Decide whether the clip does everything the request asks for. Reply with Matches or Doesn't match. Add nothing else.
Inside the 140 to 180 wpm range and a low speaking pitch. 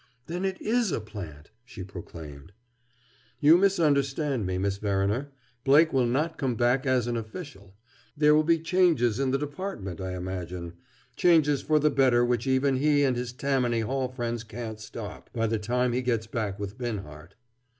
Matches